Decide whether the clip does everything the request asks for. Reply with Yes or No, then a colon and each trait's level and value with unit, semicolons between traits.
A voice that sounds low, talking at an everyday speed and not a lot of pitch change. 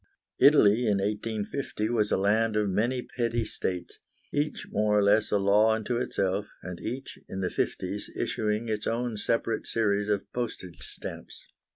Yes: low, 105 Hz; average, 160 wpm; narrow, 2.3 semitones